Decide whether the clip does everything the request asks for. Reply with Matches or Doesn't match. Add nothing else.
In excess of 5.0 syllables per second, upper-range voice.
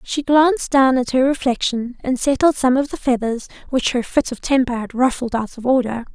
Matches